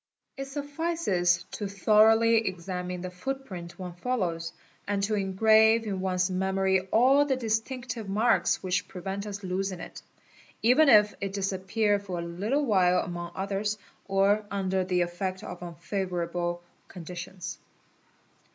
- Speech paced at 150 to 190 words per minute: No, average, 140 wpm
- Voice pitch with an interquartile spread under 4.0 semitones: Yes, average, 3.4 semitones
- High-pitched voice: Yes, high, 195 Hz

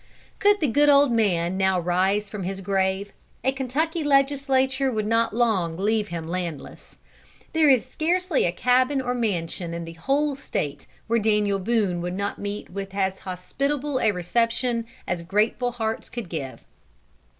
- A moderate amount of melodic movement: No, wide, 6.1 semitones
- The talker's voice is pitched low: No, high, 215 Hz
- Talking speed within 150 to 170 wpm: Yes, average, 160 wpm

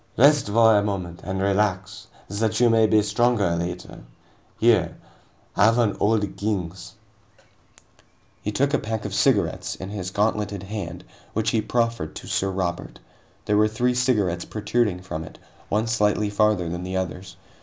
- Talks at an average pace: Yes, average, 160 wpm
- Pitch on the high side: No, low, 105 Hz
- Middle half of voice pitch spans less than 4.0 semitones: Yes, average, 3.1 semitones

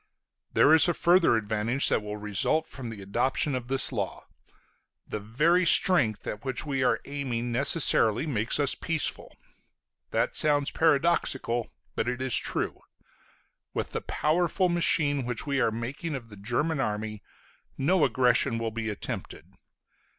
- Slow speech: No, average, 150 wpm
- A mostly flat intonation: No, average, 5.0 semitones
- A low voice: Yes, low, 130 Hz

